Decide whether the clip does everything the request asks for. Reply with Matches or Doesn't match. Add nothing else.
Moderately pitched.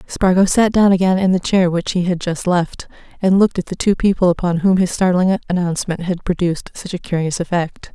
Matches